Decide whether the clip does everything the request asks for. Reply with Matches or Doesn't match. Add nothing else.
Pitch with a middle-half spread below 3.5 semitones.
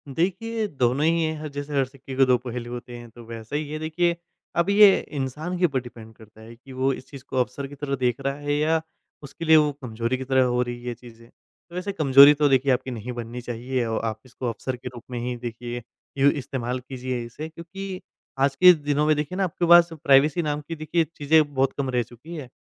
Doesn't match